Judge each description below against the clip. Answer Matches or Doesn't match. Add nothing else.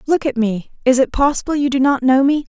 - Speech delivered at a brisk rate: Matches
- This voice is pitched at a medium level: Doesn't match